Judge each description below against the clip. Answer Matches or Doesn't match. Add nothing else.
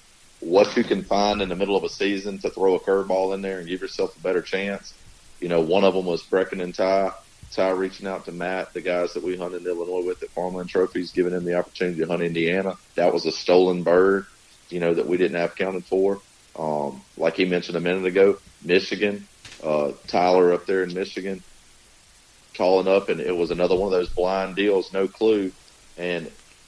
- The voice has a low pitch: Matches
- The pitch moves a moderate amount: Doesn't match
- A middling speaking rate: Doesn't match